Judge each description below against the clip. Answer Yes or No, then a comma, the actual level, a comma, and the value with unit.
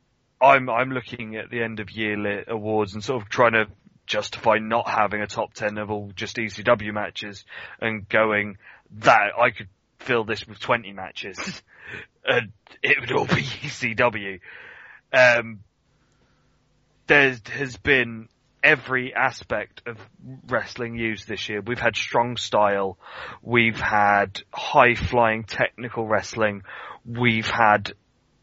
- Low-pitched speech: Yes, low, 110 Hz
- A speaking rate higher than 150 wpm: No, slow, 135 wpm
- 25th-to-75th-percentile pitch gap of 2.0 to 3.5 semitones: Yes, narrow, 2.4 semitones